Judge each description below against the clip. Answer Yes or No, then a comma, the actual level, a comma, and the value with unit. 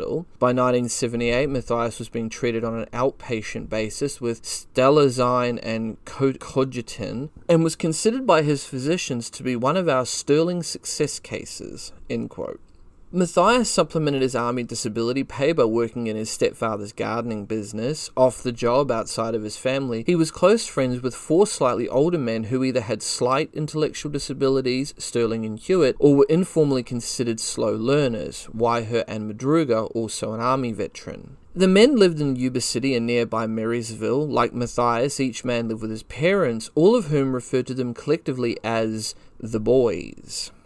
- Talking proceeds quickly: No, average, 160 wpm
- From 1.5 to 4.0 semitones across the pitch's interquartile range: Yes, average, 3.7 semitones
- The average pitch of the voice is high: No, low, 125 Hz